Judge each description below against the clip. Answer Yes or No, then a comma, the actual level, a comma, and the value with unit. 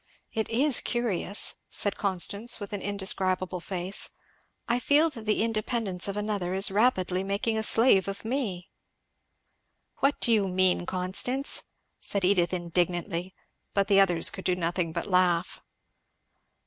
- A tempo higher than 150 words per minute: No, average, 145 wpm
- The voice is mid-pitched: No, high, 195 Hz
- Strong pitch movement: No, average, 3.3 semitones